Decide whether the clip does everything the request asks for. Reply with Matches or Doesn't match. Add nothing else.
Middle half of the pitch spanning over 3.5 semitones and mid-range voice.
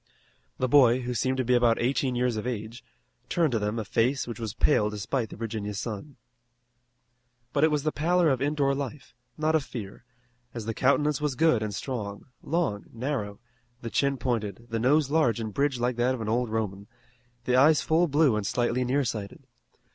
Doesn't match